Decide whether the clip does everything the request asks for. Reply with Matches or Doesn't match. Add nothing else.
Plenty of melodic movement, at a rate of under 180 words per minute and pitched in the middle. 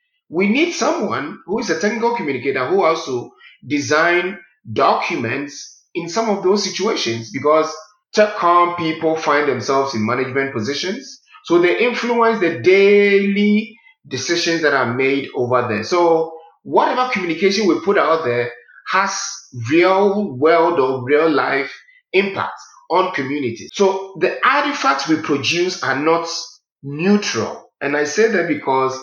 Matches